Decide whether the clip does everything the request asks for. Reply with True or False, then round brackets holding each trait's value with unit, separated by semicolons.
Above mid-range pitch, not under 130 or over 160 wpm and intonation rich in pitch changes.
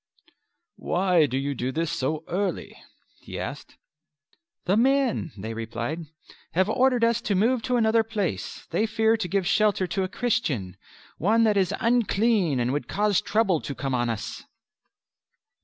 True (195 Hz; 155 wpm; 7.1 semitones)